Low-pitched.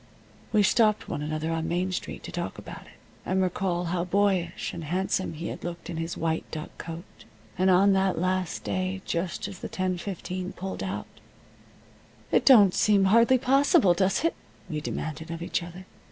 No: medium, 185 Hz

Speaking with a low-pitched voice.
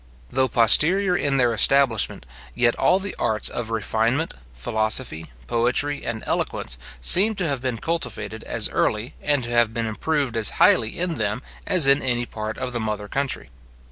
Yes: low, 120 Hz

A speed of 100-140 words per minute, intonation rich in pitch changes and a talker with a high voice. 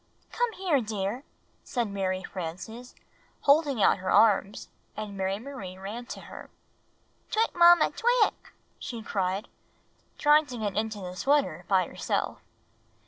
Yes: slow, 135 wpm; wide, 6.6 semitones; high, 220 Hz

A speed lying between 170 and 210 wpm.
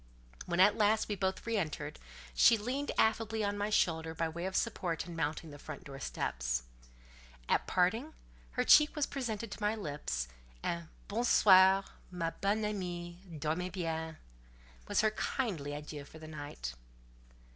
No: average, 160 wpm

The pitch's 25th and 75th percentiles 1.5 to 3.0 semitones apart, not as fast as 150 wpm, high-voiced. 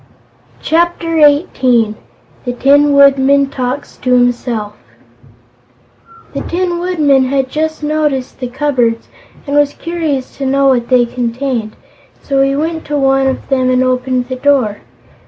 Yes: narrow, 2.6 semitones; slow, 135 wpm; very high, 270 Hz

